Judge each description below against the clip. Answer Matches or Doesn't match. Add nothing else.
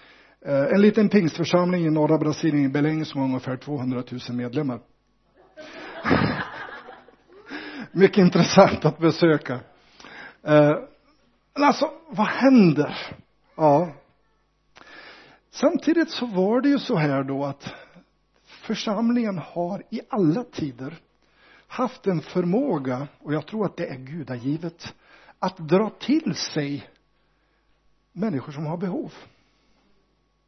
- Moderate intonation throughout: Doesn't match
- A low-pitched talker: Doesn't match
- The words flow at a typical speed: Doesn't match